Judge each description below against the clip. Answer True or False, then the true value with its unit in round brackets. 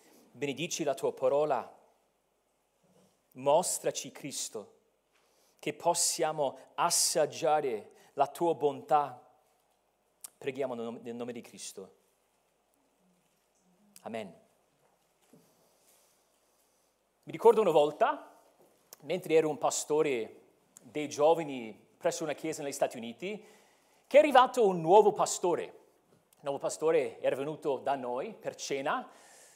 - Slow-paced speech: True (100 wpm)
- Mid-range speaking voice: True (180 Hz)